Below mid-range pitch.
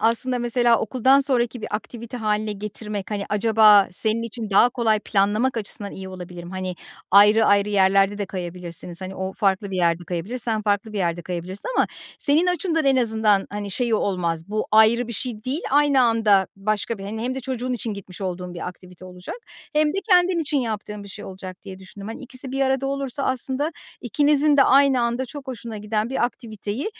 No: high, 215 Hz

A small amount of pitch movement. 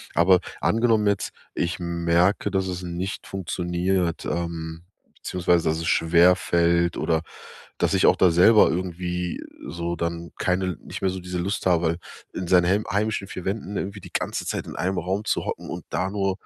Yes: narrow, 2.0 semitones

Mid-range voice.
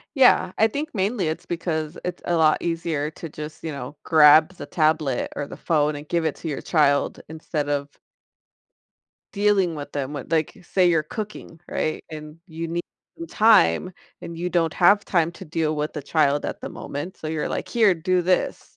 Yes: medium, 160 Hz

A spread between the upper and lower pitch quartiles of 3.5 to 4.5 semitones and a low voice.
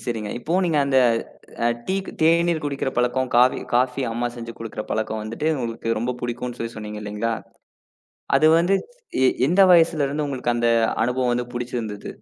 Yes: average, 4.0 semitones; low, 125 Hz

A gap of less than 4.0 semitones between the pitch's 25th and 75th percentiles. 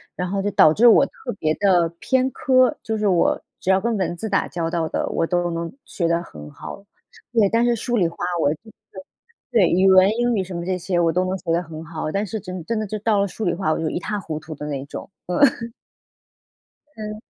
No: average, 4.4 semitones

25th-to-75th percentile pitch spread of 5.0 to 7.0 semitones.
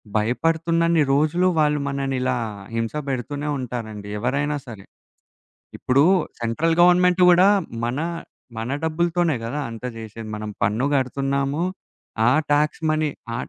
Yes: wide, 5.4 semitones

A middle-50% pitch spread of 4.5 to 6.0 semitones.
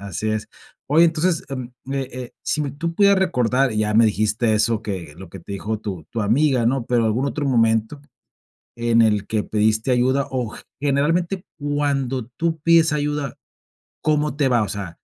Yes: average, 5.2 semitones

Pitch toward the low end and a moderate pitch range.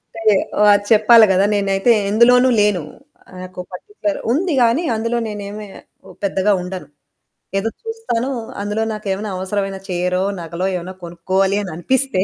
No: high, 205 Hz; average, 3.7 semitones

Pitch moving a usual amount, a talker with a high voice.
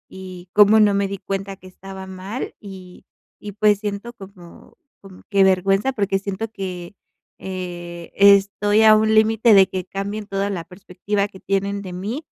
No: narrow, 1.7 semitones; high, 195 Hz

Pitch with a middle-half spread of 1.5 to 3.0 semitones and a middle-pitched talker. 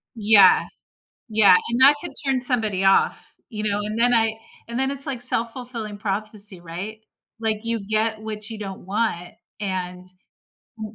No: narrow, 2.4 semitones; high, 215 Hz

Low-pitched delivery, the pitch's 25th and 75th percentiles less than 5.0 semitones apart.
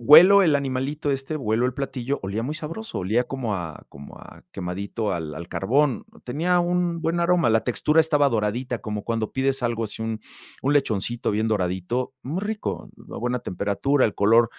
No: low, 125 Hz; wide, 5.6 semitones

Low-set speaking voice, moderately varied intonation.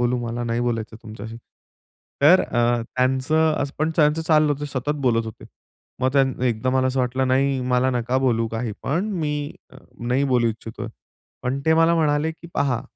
Yes: low, 130 Hz; average, 3.7 semitones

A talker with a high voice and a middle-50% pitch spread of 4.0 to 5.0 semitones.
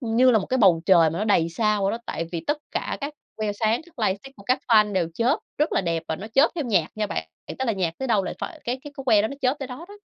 No: high, 220 Hz; wide, 5.4 semitones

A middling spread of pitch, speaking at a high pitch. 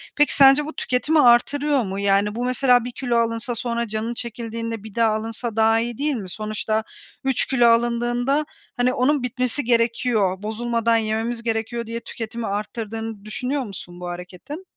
No: narrow, 2.2 semitones; high, 230 Hz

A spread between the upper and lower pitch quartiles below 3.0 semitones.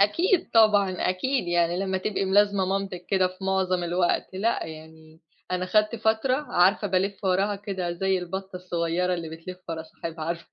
Yes: narrow, 2.4 semitones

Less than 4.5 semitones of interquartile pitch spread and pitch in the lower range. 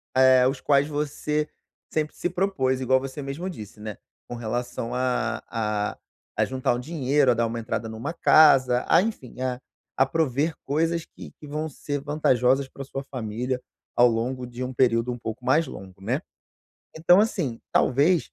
Yes: average, 3.6 semitones; low, 130 Hz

